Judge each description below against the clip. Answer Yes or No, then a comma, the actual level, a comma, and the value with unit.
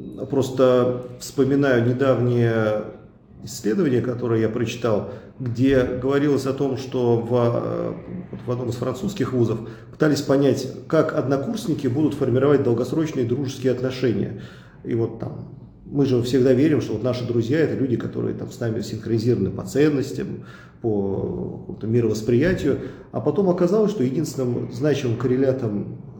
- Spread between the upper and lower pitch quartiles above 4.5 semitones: No, average, 2.7 semitones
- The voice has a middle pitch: No, low, 125 Hz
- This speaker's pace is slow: Yes, slow, 130 wpm